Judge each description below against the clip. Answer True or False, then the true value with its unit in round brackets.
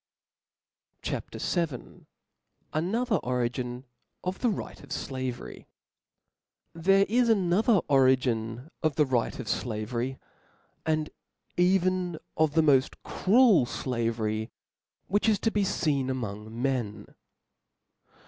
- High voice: False (140 Hz)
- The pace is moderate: False (105 wpm)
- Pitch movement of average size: False (7.1 semitones)